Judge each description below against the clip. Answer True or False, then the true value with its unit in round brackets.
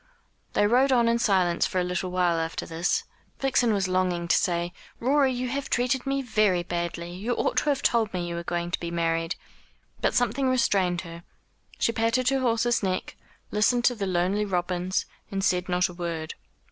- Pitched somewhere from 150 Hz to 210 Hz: True (190 Hz)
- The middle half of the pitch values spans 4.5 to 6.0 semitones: True (5.5 semitones)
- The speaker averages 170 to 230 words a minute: True (195 wpm)